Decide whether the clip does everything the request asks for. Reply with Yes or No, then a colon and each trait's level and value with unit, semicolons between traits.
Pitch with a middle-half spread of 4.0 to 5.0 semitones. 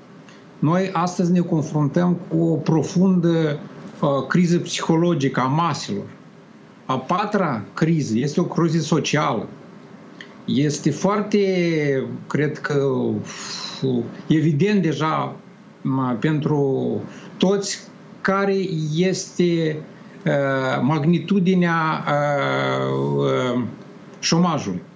Yes: average, 4.5 semitones